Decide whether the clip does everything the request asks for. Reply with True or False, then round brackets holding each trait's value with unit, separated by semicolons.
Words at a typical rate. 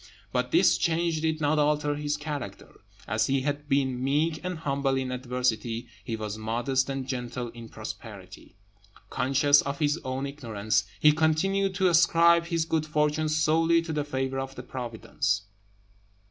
True (155 wpm)